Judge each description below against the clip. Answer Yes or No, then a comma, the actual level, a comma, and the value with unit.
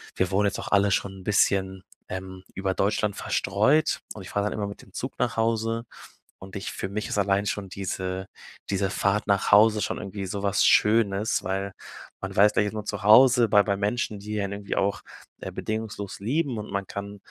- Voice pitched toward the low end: Yes, low, 100 Hz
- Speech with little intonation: Yes, narrow, 1.6 semitones